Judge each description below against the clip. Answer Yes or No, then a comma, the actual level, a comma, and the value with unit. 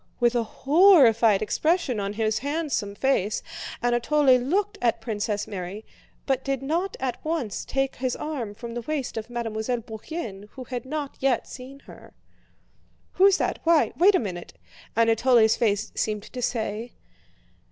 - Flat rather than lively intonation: No, average, 4.2 semitones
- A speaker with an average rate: Yes, average, 150 wpm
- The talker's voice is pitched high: Yes, high, 245 Hz